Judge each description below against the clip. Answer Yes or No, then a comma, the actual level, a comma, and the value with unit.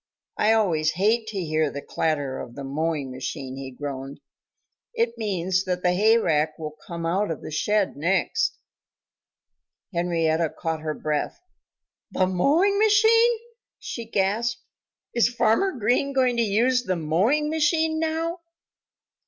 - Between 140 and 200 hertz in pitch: Yes, high, 190 Hz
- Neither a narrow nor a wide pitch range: No, wide, 8.0 semitones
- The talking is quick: No, average, 140 wpm